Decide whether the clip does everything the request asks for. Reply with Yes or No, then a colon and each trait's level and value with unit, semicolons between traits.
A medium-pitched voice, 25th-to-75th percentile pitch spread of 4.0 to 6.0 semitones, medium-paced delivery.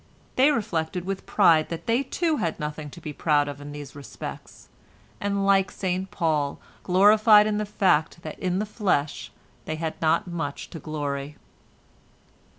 Yes: medium, 170 Hz; average, 4.9 semitones; average, 160 wpm